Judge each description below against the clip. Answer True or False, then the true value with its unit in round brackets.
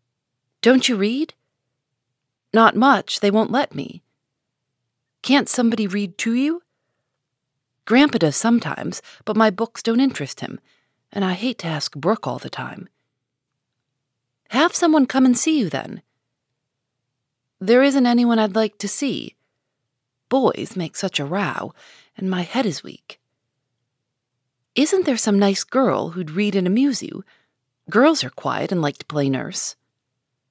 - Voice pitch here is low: False (190 Hz)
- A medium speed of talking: True (145 wpm)